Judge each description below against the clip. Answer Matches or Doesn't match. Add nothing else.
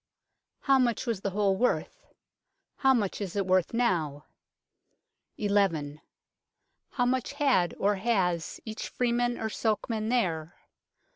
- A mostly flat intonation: Doesn't match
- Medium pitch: Doesn't match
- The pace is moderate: Doesn't match